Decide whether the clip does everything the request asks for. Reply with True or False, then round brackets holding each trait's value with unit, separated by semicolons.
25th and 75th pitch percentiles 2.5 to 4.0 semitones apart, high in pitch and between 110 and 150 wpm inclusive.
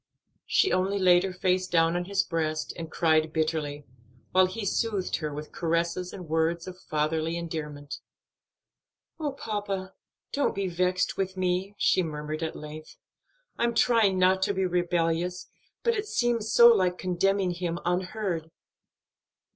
False (2.9 semitones; 180 Hz; 145 wpm)